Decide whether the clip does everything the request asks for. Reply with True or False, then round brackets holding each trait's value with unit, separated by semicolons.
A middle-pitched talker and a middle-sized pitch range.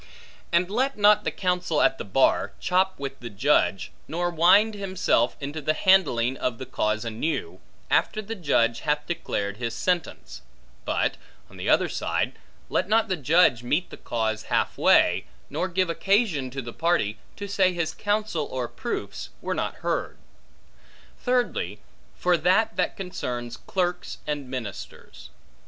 False (165 Hz; 7.4 semitones)